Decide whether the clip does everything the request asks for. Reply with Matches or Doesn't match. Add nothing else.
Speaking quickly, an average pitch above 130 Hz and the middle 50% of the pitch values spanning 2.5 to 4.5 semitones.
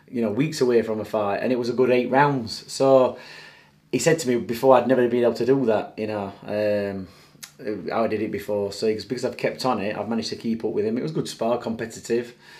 Doesn't match